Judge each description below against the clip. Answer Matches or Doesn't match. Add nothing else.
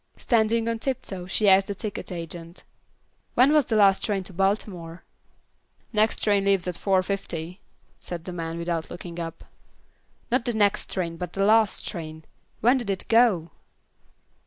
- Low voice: Doesn't match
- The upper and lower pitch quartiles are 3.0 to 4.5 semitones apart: Matches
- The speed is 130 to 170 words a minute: Matches